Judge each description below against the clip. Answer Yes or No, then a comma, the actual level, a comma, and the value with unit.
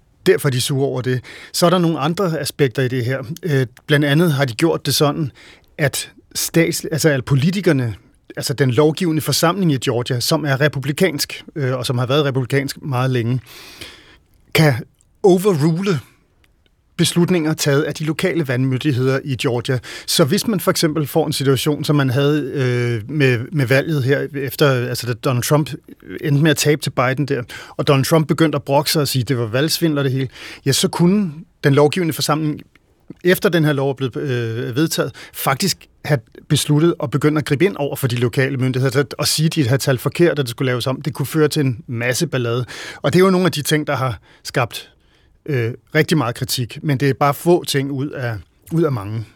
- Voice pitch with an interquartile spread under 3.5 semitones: Yes, average, 3.1 semitones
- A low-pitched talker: No, medium, 145 Hz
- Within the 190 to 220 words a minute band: Yes, average, 205 wpm